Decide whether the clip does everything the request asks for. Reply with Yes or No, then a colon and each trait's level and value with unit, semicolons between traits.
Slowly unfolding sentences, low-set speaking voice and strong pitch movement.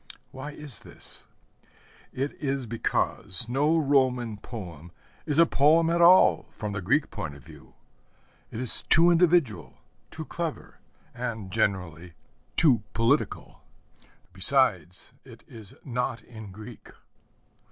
Yes: slow, 120 wpm; low, 125 Hz; wide, 6.3 semitones